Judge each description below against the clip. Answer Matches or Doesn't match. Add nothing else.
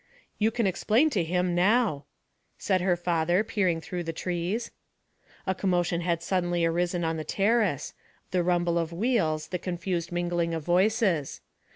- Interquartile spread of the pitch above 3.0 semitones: Doesn't match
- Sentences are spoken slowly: Doesn't match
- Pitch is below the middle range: Doesn't match